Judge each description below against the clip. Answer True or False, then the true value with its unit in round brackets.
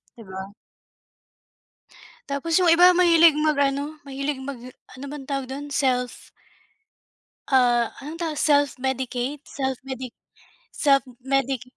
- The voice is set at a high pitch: True (275 Hz)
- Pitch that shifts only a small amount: True (2.3 semitones)